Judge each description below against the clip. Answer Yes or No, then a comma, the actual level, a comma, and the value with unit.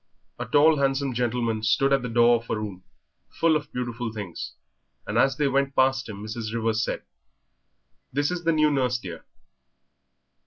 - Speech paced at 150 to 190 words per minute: Yes, average, 170 wpm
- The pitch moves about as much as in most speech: Yes, average, 3.6 semitones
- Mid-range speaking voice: No, low, 125 Hz